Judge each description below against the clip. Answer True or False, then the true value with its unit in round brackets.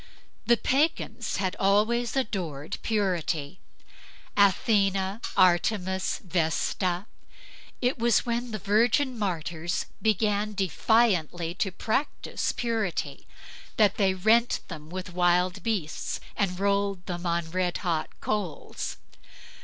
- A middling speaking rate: False (105 wpm)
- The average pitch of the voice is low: False (195 Hz)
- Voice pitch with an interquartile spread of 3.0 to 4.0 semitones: True (3.6 semitones)